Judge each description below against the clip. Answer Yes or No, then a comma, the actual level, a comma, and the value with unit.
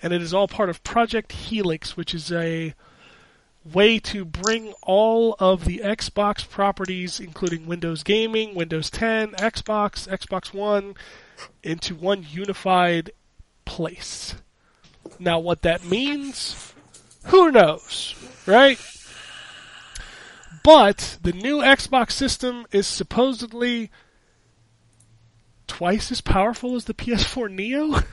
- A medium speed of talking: No, slow, 110 wpm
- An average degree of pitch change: Yes, average, 4.8 semitones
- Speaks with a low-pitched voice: No, high, 200 Hz